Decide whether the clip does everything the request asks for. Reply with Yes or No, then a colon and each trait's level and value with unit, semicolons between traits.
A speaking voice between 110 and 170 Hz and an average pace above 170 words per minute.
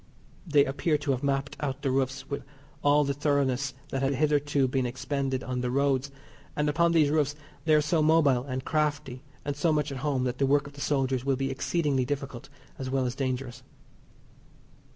Yes: medium, 140 Hz; average, 195 wpm